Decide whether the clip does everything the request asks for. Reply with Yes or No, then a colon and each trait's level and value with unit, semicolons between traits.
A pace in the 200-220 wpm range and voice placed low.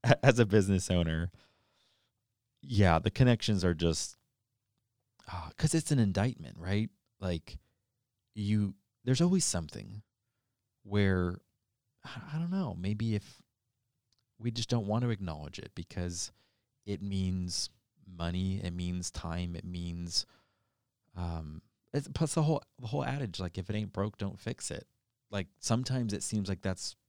No: average, 140 wpm; low, 105 Hz